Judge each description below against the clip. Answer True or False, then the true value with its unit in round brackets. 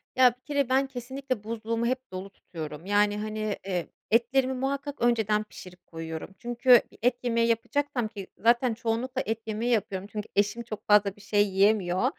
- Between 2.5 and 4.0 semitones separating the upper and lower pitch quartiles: True (3.4 semitones)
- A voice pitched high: True (225 Hz)